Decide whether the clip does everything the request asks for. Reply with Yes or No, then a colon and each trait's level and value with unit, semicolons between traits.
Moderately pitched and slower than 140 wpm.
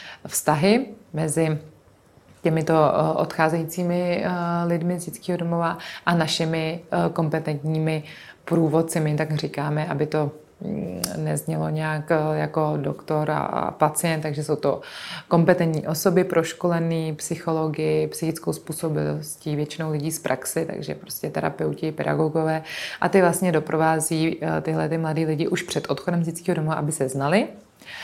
Yes: medium, 160 Hz; average, 120 wpm